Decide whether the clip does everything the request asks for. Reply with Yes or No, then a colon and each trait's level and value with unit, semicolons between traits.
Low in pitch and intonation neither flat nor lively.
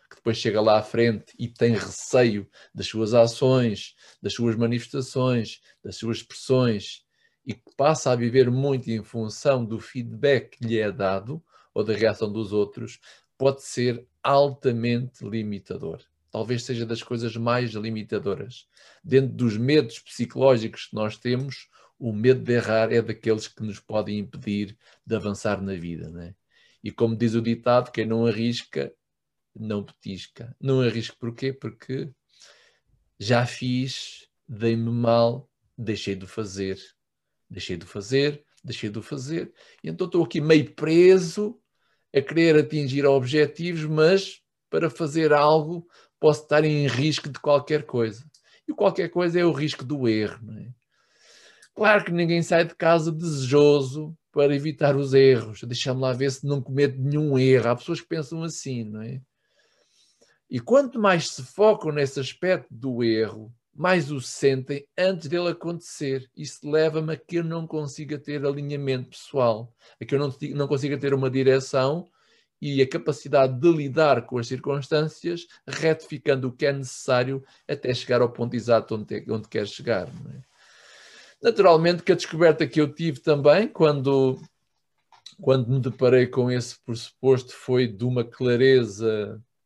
Yes: low, 130 Hz; average, 4.6 semitones